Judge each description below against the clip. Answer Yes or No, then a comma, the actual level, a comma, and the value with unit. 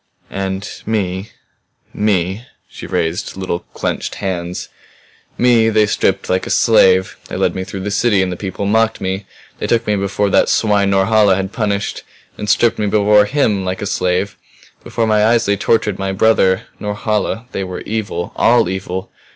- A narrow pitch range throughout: Yes, narrow, 2.3 semitones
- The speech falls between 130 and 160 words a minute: No, average, 170 wpm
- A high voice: No, low, 100 Hz